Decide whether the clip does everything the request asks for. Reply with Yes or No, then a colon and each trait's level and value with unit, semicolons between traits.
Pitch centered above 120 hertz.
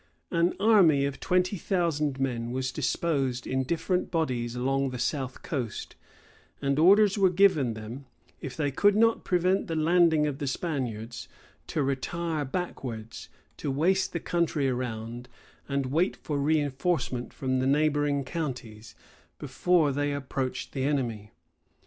Yes: medium, 140 Hz